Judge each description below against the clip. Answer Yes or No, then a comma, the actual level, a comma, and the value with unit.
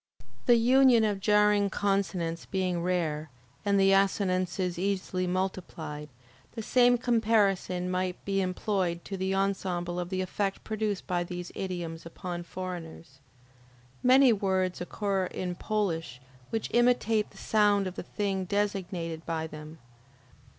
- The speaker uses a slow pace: Yes, slow, 130 wpm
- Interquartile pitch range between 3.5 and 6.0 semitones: No, average, 2.7 semitones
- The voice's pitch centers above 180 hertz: Yes, high, 190 Hz